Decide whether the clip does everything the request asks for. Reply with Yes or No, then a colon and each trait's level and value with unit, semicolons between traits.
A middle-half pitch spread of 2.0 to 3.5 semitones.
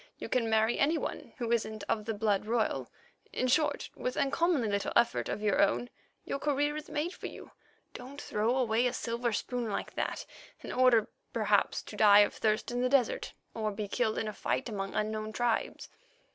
Yes: average, 2.9 semitones